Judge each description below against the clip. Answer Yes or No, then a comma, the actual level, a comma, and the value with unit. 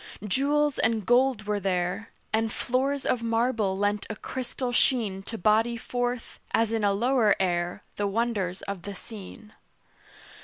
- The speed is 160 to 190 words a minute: No, average, 150 wpm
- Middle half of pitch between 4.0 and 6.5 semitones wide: No, average, 3.5 semitones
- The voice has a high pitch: Yes, high, 220 Hz